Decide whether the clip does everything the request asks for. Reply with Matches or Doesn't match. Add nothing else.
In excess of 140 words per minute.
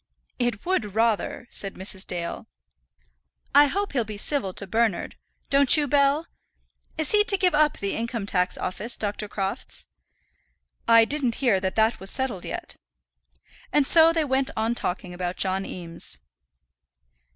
Matches